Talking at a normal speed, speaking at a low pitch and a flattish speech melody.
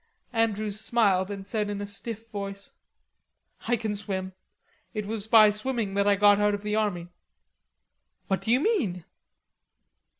No: average, 155 wpm; high, 205 Hz; narrow, 1.8 semitones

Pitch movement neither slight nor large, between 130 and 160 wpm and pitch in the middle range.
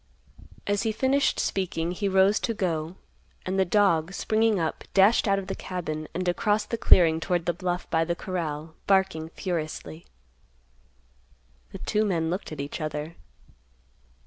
Yes: average, 3.6 semitones; average, 155 wpm; medium, 180 Hz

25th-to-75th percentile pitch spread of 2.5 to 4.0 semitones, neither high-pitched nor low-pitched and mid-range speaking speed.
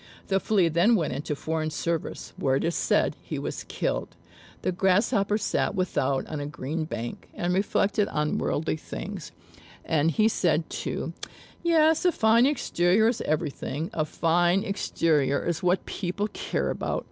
No: average, 4.6 semitones; medium, 175 Hz; average, 160 wpm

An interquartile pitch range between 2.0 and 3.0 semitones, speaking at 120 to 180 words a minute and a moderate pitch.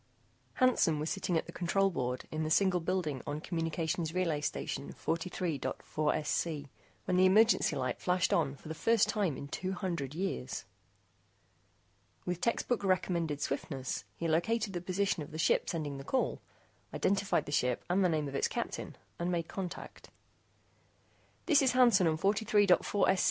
No: average, 4.0 semitones; average, 160 wpm; medium, 170 Hz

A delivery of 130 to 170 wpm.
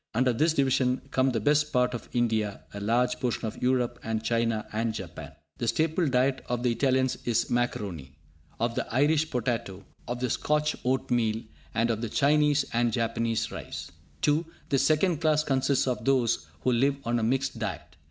No: average, 180 wpm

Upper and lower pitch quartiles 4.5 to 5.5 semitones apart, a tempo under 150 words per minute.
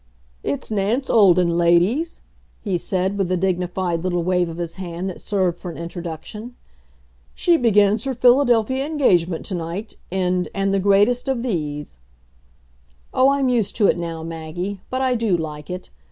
No: average, 4.9 semitones; average, 165 wpm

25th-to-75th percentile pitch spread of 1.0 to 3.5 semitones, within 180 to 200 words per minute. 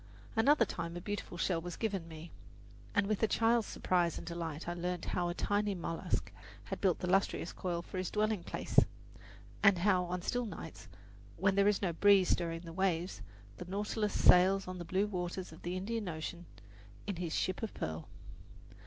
Yes: average, 2.9 semitones; average, 190 wpm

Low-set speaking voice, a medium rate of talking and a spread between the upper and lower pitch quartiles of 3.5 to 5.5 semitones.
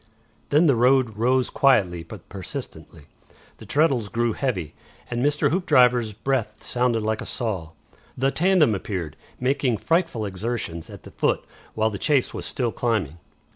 Yes: low, 120 Hz; average, 150 wpm; average, 4.6 semitones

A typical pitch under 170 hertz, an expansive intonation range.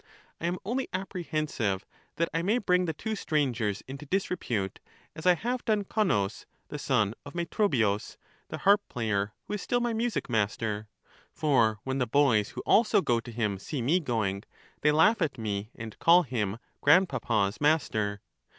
Yes: medium, 140 Hz; wide, 8.9 semitones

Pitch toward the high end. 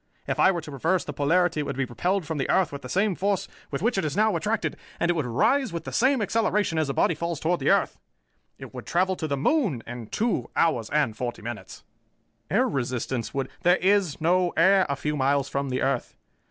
No: medium, 160 Hz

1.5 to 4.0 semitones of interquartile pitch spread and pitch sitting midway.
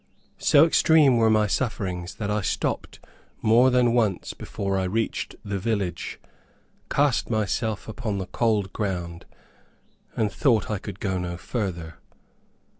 No: average, 3.5 semitones; low, 105 Hz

